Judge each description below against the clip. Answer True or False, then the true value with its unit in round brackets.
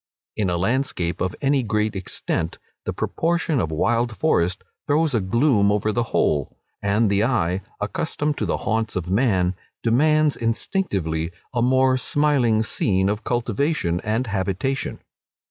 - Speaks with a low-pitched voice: True (110 Hz)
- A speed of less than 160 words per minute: True (145 wpm)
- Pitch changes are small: False (5.6 semitones)